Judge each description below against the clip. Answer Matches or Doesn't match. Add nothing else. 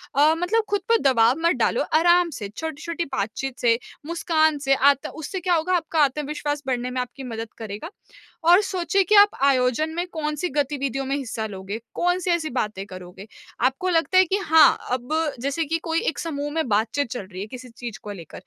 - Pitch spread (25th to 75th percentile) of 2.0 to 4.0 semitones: Doesn't match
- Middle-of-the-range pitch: Doesn't match